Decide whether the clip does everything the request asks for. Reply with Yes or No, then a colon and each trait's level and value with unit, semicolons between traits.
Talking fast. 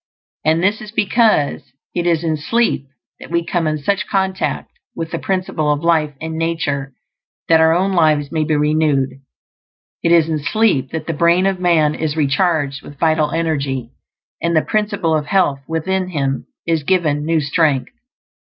No: average, 170 wpm